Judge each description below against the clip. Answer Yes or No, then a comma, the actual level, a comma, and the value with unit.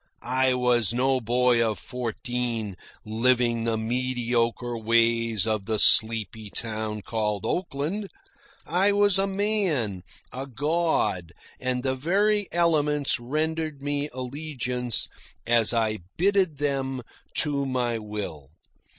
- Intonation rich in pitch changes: No, average, 4.5 semitones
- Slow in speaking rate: Yes, slow, 115 wpm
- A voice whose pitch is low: Yes, low, 125 Hz